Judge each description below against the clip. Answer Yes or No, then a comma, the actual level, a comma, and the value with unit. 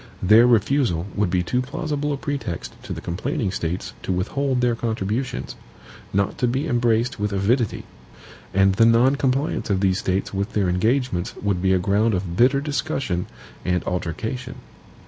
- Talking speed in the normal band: Yes, average, 165 wpm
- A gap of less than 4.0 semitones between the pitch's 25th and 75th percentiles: No, average, 5.3 semitones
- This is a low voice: Yes, low, 110 Hz